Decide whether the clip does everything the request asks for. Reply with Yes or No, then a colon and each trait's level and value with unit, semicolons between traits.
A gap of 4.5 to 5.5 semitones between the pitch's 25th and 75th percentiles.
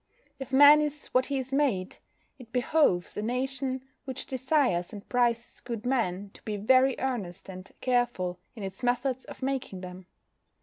Yes: average, 4.9 semitones